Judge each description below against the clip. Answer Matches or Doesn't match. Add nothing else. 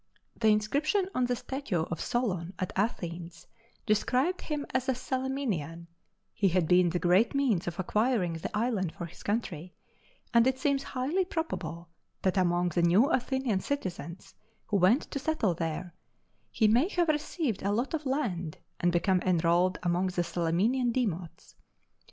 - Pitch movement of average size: Doesn't match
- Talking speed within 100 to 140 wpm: Doesn't match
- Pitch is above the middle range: Matches